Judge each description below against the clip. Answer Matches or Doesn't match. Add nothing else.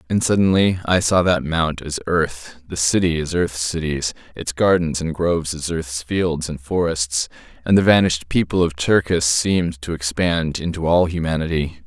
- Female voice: Doesn't match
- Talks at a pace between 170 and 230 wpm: Doesn't match